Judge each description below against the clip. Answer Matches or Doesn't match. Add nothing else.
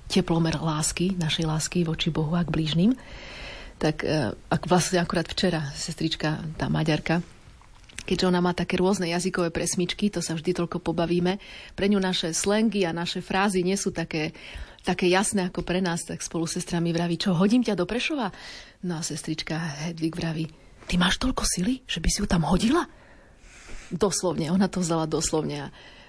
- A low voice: Doesn't match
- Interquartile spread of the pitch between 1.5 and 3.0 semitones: Matches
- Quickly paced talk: Matches